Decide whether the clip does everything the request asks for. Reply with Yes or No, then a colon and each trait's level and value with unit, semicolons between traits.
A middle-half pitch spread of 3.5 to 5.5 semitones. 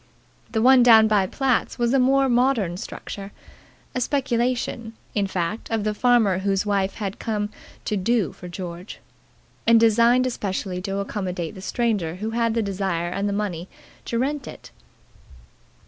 Yes: average, 3.8 semitones